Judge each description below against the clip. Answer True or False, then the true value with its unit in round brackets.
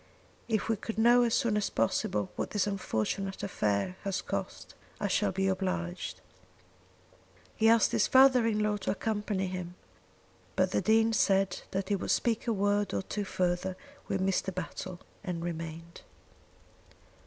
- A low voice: False (195 Hz)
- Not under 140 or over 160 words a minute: True (155 wpm)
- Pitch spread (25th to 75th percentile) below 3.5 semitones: True (2.8 semitones)